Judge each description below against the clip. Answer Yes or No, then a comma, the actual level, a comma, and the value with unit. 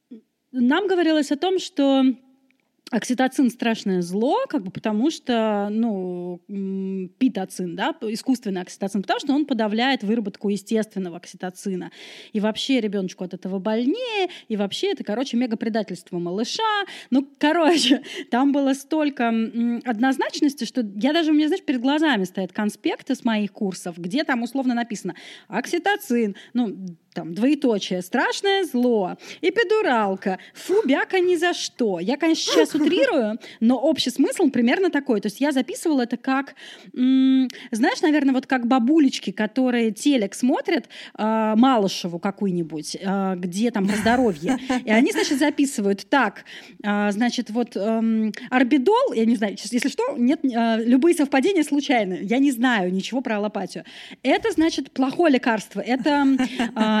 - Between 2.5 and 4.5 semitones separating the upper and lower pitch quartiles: No, wide, 5.5 semitones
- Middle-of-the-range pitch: No, high, 245 Hz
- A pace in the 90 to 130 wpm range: No, average, 140 wpm